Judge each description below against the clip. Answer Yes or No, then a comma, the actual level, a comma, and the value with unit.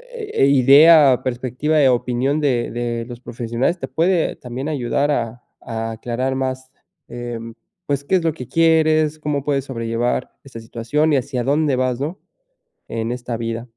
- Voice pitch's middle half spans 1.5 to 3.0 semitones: No, average, 3.6 semitones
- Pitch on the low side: Yes, low, 130 Hz